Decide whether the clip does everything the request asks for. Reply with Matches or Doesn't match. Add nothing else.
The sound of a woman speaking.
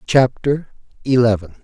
Doesn't match